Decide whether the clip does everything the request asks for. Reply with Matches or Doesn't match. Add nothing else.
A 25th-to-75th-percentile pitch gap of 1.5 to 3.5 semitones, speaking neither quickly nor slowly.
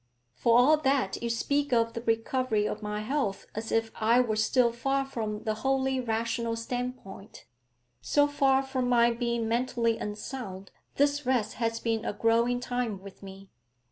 Matches